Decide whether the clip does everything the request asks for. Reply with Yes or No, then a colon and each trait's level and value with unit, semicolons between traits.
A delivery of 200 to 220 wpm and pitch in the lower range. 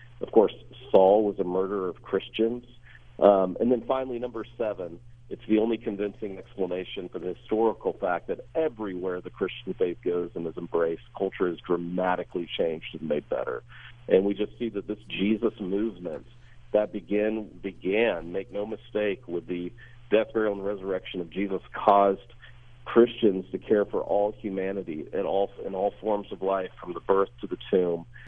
No: average, 170 wpm; low, 105 Hz